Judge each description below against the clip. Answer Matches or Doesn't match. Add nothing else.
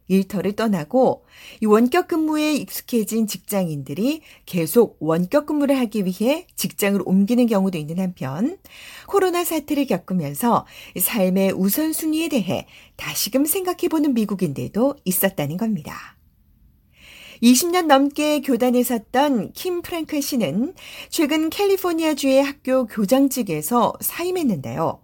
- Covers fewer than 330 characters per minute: Matches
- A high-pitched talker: Matches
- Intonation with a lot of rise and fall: Matches